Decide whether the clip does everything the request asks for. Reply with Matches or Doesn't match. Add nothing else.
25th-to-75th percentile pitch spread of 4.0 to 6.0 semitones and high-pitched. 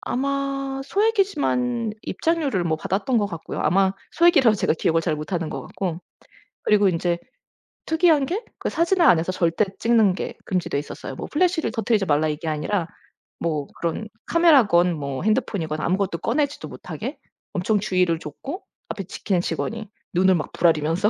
Doesn't match